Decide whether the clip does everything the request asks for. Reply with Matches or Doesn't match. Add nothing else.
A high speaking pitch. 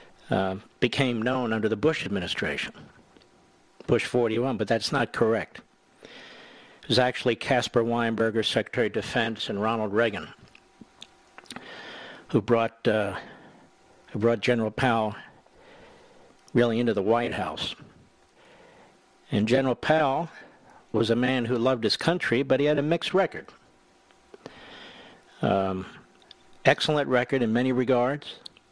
Doesn't match